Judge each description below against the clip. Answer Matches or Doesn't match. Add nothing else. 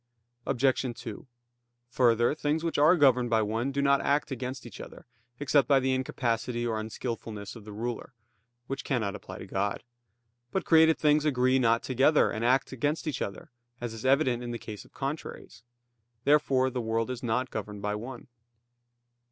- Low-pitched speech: Matches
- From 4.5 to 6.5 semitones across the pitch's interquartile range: Doesn't match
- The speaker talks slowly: Doesn't match